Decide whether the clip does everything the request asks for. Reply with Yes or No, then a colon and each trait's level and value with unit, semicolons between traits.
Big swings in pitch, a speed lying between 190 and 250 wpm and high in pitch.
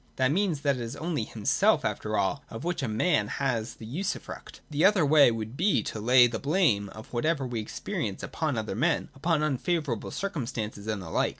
No: wide, 6.2 semitones; average, 200 wpm; low, 130 Hz